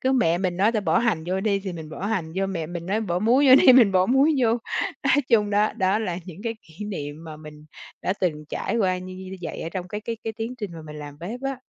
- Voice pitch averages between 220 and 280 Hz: No, high, 190 Hz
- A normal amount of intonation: Yes, average, 4.8 semitones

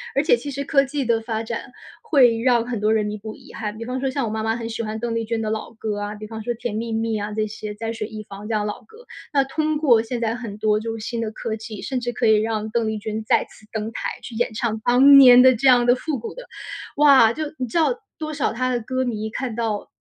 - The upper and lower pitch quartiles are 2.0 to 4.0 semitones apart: Yes, average, 2.7 semitones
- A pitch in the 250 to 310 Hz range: No, high, 230 Hz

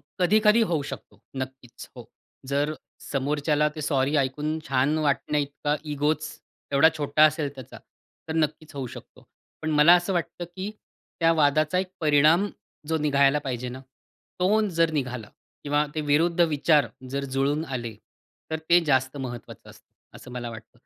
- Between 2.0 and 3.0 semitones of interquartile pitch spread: Yes, narrow, 2.6 semitones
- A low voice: No, medium, 150 Hz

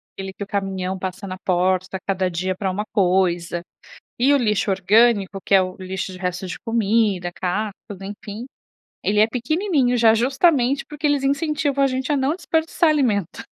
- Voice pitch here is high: Yes, high, 205 Hz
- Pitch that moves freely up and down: Yes, wide, 5.9 semitones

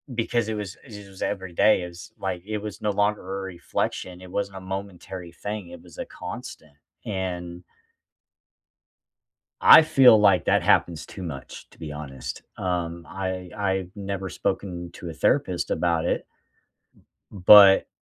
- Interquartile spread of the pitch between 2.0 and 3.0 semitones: Yes, average, 2.7 semitones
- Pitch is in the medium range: No, very low, 95 Hz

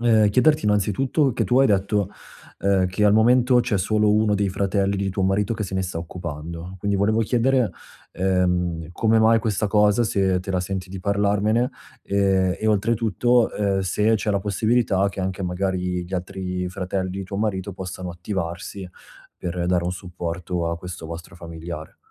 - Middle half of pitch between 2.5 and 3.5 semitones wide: Yes, average, 2.8 semitones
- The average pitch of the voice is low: Yes, very low, 95 Hz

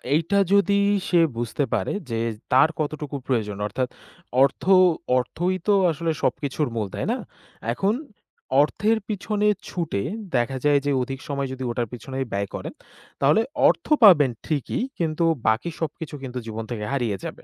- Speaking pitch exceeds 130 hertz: Yes, medium, 140 Hz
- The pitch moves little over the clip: No, wide, 5.5 semitones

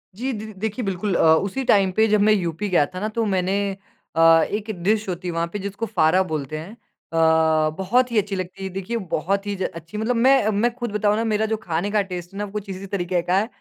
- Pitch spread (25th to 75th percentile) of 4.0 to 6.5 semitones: No, average, 3.2 semitones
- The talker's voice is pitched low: No, high, 195 Hz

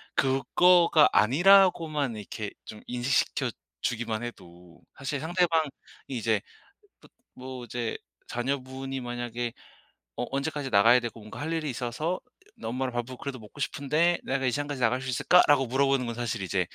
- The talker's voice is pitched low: Yes, low, 130 Hz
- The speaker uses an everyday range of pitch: Yes, average, 3.5 semitones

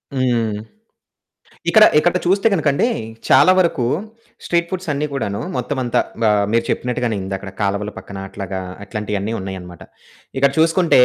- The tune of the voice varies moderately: No, wide, 8.2 semitones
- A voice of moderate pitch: No, low, 120 Hz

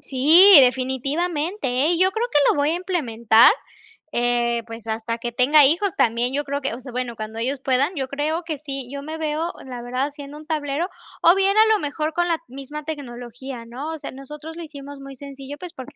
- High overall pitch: Yes, very high, 280 Hz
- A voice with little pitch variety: No, average, 4.0 semitones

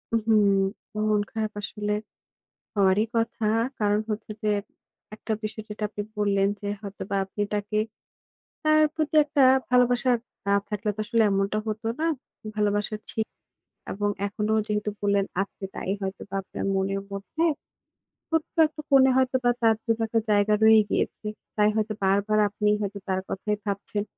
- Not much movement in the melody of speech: Yes, narrow, 1.9 semitones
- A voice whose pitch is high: Yes, high, 210 Hz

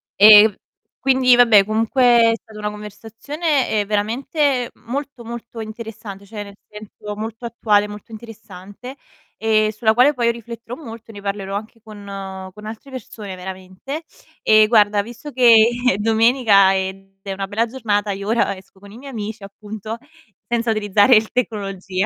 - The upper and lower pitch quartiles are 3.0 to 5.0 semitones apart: No, narrow, 2.5 semitones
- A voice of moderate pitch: No, high, 220 Hz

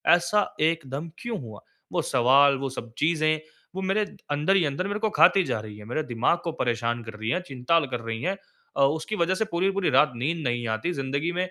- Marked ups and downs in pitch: Yes, wide, 6.3 semitones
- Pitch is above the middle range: No, medium, 150 Hz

